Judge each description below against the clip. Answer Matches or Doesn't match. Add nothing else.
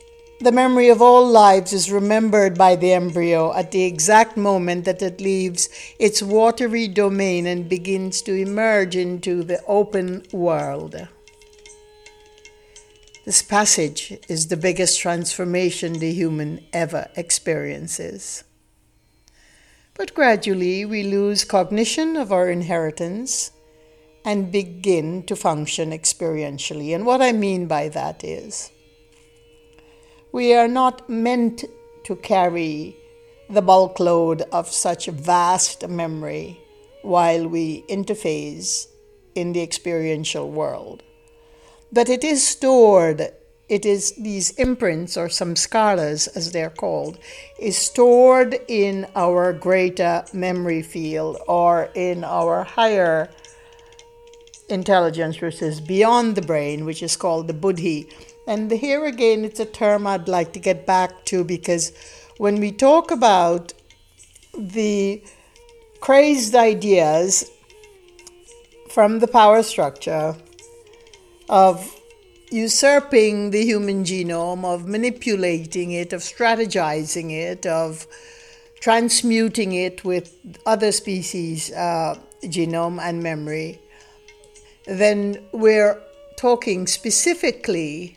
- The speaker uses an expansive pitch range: Matches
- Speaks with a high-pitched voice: Matches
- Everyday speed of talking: Doesn't match